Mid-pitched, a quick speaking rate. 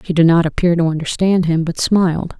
Yes: medium, 170 Hz; fast, 225 wpm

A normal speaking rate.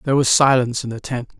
No: fast, 260 wpm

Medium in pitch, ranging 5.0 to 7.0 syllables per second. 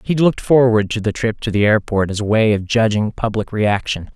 No: low, 110 Hz; 5.5 syllables/s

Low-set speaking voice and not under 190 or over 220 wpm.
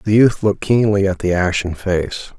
Yes: low, 100 Hz; average, 200 wpm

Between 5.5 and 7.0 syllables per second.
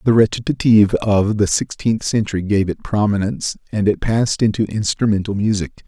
Yes: 5.7 syllables/s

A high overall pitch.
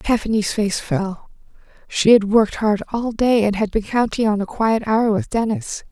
Yes: high, 215 Hz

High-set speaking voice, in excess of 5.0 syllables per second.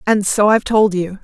Yes: high, 205 Hz; 5.5 syllables/s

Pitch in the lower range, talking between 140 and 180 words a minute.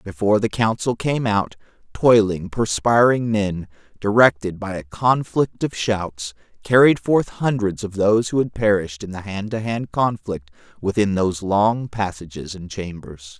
Yes: low, 105 Hz; average, 150 wpm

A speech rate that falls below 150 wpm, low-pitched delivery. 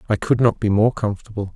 No: fast, 230 wpm; low, 105 Hz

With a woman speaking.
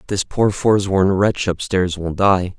No: male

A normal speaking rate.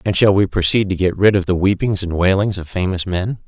No: fast, 260 wpm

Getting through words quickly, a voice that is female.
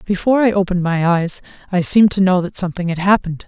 Yes: fast, 225 wpm; female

